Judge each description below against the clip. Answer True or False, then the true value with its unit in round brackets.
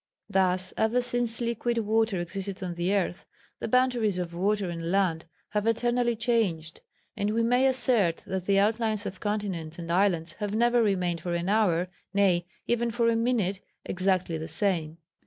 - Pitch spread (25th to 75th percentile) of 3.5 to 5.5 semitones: True (4.4 semitones)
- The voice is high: True (200 Hz)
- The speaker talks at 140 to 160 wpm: False (170 wpm)